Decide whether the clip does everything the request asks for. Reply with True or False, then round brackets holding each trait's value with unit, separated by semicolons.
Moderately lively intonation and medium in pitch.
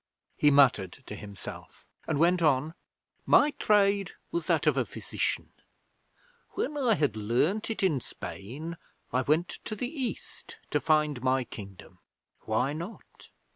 False (7.8 semitones; 155 Hz)